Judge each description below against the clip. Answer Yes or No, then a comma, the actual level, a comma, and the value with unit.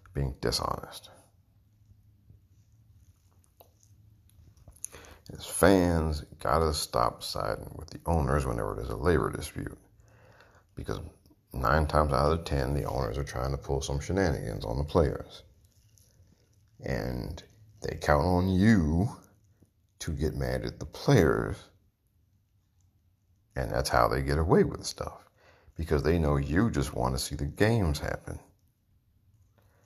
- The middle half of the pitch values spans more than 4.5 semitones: Yes, average, 4.9 semitones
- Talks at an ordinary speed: No, slow, 125 wpm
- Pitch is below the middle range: Yes, very low, 95 Hz